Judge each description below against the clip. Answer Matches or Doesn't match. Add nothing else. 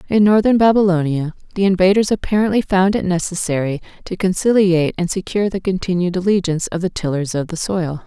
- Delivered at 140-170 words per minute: Matches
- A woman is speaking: Matches